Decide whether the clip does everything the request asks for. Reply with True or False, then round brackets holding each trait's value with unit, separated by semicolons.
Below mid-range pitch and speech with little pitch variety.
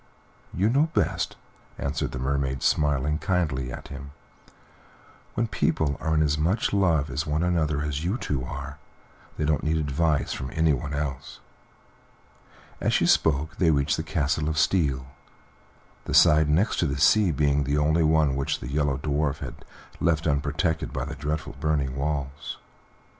True (75 Hz; 2.1 semitones)